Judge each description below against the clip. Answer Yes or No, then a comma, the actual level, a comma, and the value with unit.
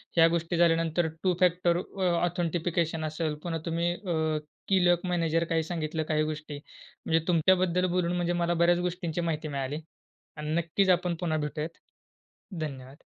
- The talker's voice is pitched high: No, medium, 170 Hz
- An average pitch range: No, narrow, 1.9 semitones